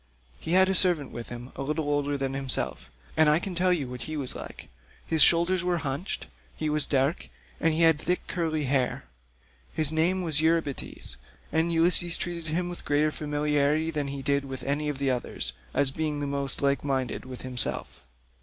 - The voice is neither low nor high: Yes, medium, 150 Hz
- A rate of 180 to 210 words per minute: Yes, average, 190 wpm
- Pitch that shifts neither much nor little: Yes, average, 3.1 semitones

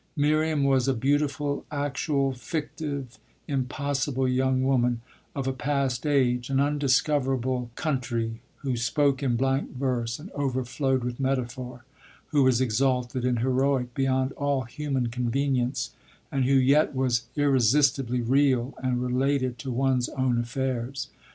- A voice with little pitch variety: Yes, narrow, 2.0 semitones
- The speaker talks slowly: Yes, slow, 130 wpm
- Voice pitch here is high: No, low, 130 Hz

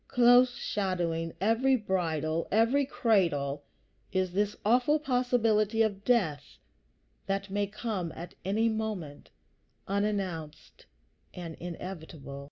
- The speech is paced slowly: Yes, slow, 100 wpm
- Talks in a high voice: Yes, high, 200 Hz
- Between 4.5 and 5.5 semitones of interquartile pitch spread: Yes, average, 5.1 semitones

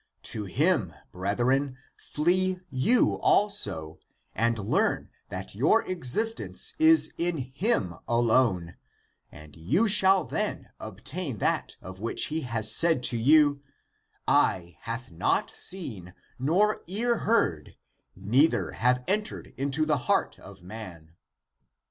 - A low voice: Yes, low, 130 Hz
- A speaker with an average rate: No, slow, 120 wpm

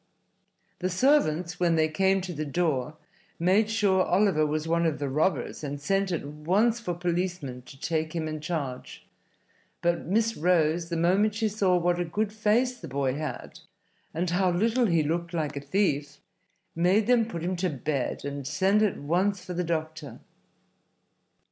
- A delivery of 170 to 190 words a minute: Yes, average, 175 wpm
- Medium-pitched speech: Yes, medium, 175 Hz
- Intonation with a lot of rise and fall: No, average, 3.9 semitones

